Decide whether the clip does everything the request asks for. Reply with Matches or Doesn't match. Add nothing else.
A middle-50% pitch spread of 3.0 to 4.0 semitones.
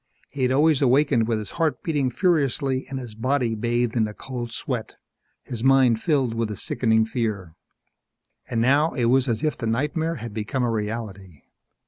Matches